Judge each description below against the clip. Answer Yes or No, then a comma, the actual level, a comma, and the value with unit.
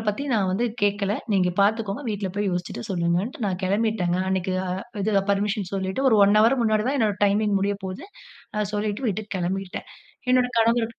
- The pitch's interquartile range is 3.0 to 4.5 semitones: No, narrow, 2.5 semitones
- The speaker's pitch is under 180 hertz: No, high, 205 Hz